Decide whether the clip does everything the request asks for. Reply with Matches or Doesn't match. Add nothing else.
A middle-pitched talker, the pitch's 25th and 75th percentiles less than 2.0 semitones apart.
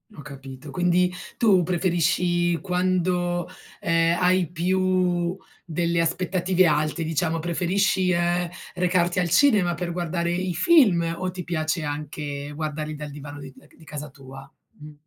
Doesn't match